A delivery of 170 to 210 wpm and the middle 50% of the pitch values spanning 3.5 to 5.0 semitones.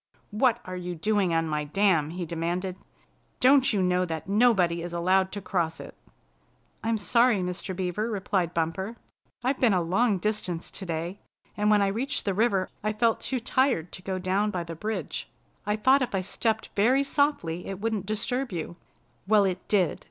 Yes: average, 180 wpm; average, 3.8 semitones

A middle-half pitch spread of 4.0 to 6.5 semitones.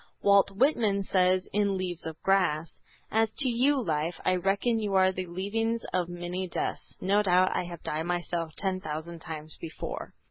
No: average, 2.7 semitones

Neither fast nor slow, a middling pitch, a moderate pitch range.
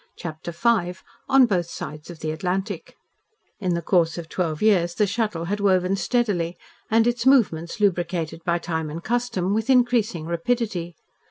Yes: average, 160 wpm; medium, 180 Hz; average, 4.5 semitones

